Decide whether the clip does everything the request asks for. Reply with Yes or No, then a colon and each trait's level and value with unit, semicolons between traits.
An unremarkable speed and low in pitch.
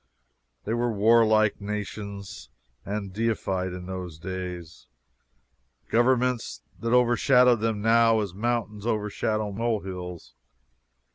No: slow, 100 wpm; low, 105 Hz